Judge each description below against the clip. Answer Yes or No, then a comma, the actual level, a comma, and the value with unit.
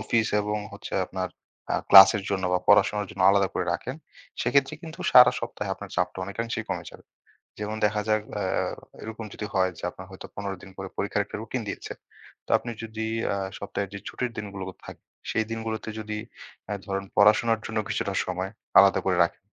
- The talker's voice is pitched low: Yes, low, 105 Hz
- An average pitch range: No, narrow, 2.2 semitones